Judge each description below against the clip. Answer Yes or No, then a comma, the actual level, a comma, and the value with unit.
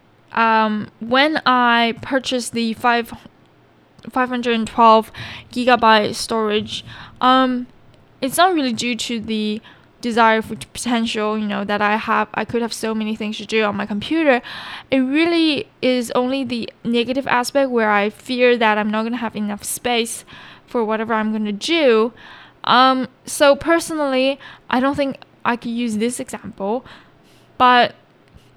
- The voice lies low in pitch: No, high, 235 Hz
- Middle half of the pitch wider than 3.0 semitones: No, average, 2.7 semitones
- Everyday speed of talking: Yes, average, 150 wpm